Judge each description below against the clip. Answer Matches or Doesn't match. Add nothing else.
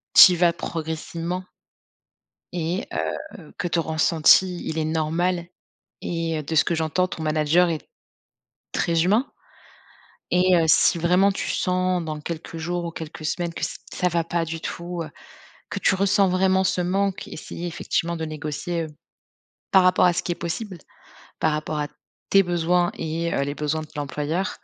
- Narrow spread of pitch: Matches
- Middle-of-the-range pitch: Matches